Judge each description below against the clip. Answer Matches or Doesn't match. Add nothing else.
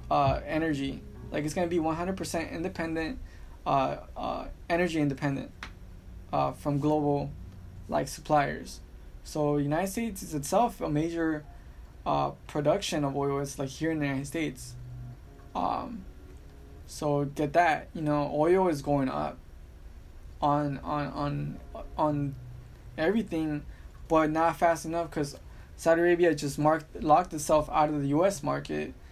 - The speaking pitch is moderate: Matches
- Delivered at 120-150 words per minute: Matches